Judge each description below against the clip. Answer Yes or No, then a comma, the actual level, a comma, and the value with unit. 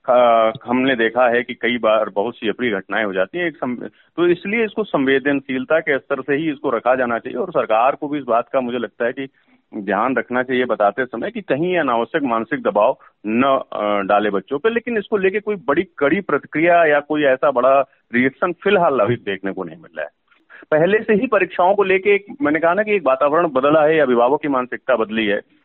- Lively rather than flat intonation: Yes, wide, 6.7 semitones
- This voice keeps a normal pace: No, fast, 215 wpm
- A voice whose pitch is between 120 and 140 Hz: Yes, low, 135 Hz